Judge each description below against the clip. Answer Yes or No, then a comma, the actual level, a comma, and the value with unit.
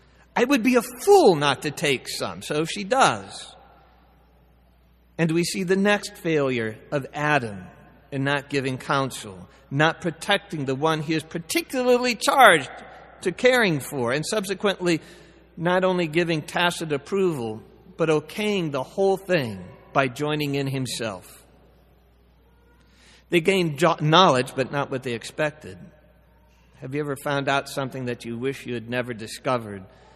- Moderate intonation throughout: No, wide, 6.0 semitones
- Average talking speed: Yes, average, 145 wpm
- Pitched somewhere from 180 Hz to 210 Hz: No, medium, 150 Hz